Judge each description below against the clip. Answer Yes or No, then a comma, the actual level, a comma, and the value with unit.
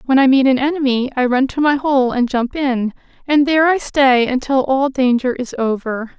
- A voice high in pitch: Yes, very high, 265 Hz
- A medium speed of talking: No, fast, 215 wpm